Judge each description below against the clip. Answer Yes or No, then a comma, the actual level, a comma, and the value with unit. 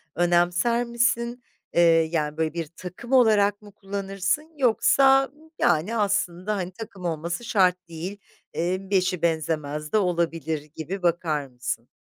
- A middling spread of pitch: Yes, average, 4.2 semitones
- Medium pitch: Yes, medium, 180 Hz